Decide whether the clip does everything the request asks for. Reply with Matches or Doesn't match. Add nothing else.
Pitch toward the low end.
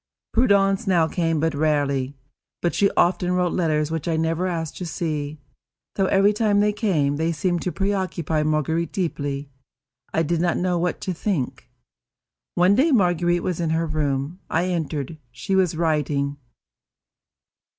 Doesn't match